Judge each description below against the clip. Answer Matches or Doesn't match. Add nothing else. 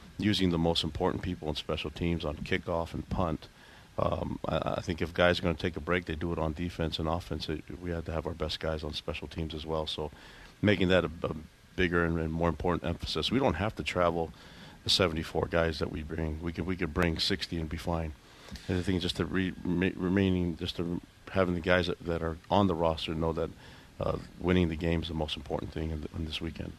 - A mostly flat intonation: Matches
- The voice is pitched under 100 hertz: Matches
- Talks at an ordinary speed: Doesn't match